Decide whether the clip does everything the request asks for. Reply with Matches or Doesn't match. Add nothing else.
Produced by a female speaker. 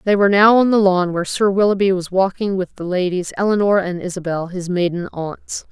Matches